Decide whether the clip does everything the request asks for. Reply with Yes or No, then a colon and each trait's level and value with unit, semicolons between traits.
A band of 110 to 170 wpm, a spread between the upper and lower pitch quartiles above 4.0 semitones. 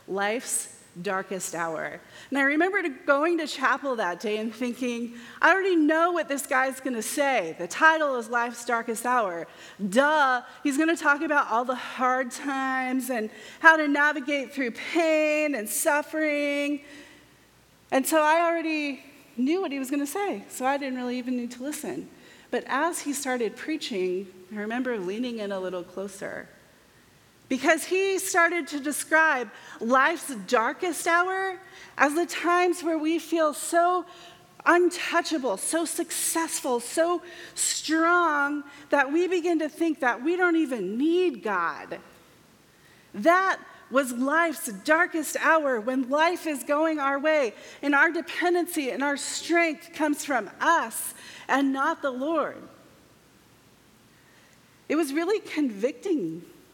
Yes: average, 145 wpm; average, 4.5 semitones